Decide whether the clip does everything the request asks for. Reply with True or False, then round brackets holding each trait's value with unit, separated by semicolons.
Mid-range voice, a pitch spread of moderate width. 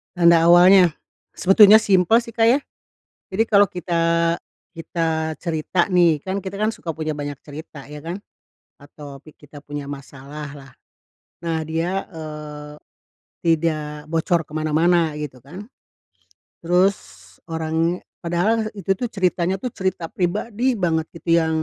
True (170 Hz; 3.5 semitones)